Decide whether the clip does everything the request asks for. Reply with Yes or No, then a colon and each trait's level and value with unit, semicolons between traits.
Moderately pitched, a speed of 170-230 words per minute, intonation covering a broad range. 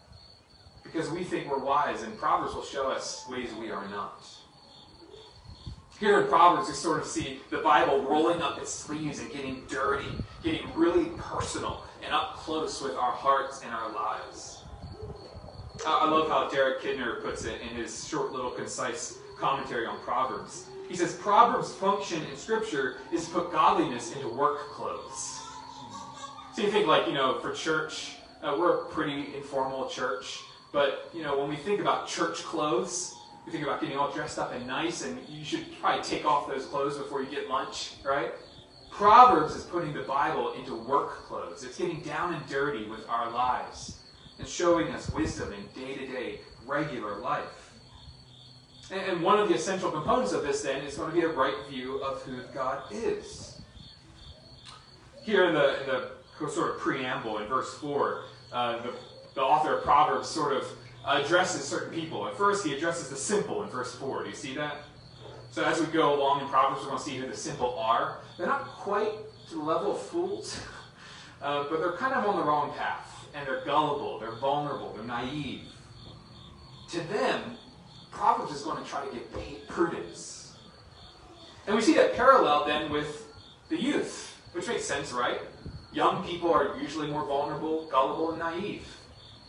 Yes: medium, 150 Hz; average, 180 wpm; wide, 6.8 semitones